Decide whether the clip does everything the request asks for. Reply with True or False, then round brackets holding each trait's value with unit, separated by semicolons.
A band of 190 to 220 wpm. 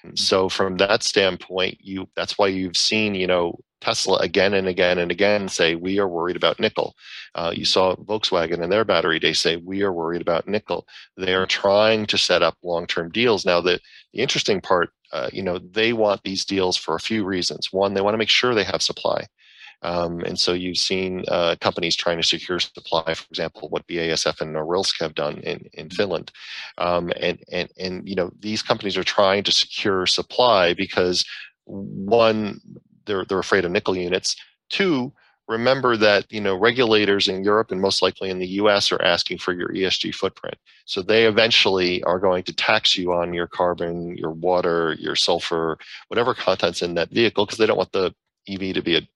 True (200 wpm)